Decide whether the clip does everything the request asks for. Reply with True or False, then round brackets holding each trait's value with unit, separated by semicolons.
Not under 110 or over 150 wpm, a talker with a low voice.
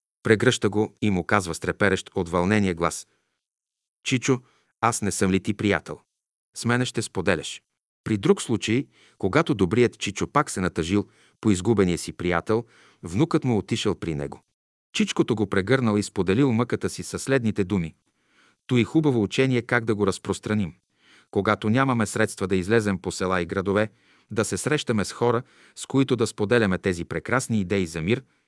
False (165 wpm; 105 Hz)